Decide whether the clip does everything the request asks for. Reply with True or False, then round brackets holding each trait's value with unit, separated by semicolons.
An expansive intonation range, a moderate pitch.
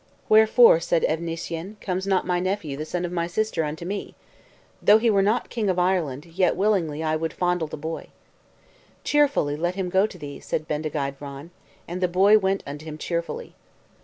False (3.7 semitones; 175 Hz)